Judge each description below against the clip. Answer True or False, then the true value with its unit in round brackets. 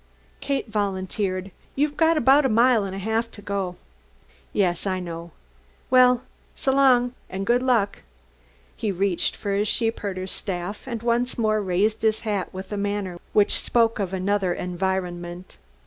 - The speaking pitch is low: False (205 Hz)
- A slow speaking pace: False (150 wpm)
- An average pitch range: True (3.9 semitones)